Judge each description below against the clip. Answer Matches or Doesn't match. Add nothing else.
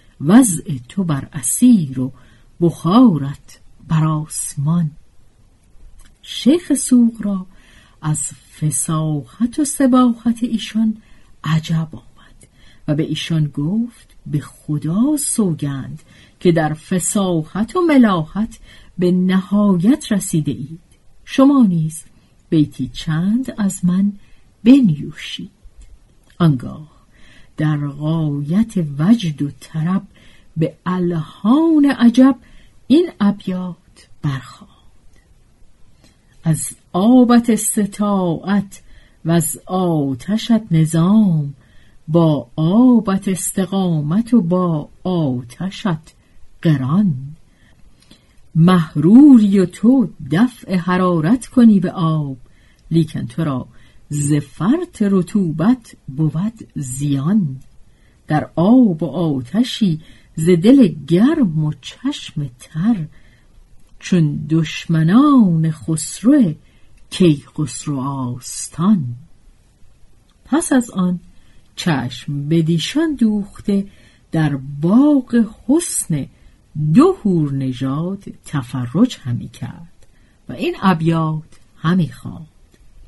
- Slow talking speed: Matches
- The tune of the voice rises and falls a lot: Matches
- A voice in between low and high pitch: Matches